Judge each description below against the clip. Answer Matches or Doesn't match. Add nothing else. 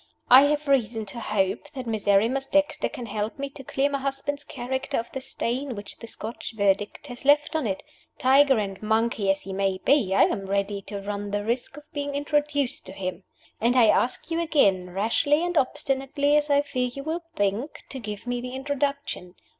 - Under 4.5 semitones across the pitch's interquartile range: Doesn't match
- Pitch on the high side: Matches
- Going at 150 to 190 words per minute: Doesn't match